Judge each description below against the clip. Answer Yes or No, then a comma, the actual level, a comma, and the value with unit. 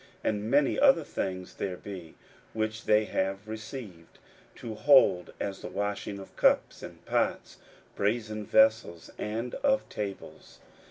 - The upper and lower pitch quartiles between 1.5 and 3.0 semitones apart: Yes, narrow, 2.4 semitones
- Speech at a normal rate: No, slow, 130 wpm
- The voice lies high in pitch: No, low, 105 Hz